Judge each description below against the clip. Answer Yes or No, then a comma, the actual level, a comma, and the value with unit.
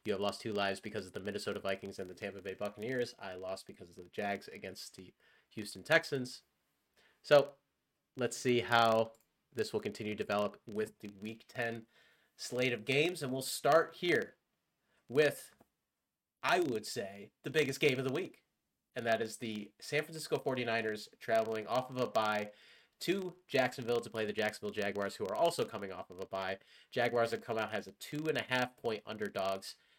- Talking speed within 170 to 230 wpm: Yes, average, 190 wpm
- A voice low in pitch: Yes, low, 115 Hz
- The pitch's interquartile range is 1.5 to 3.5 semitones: No, average, 4.1 semitones